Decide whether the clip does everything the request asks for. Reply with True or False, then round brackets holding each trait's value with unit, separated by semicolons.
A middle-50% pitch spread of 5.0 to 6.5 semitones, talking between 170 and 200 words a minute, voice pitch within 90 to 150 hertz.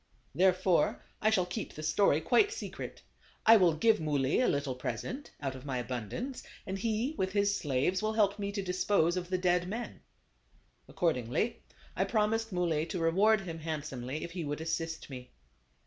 False (5.5 semitones; 175 wpm; 180 Hz)